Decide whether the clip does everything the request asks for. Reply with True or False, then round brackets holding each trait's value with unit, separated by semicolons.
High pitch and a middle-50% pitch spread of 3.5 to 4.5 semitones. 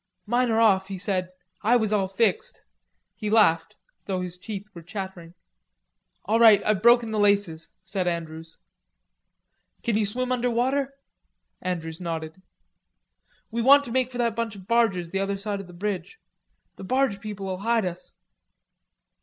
True (200 Hz; 4.1 semitones)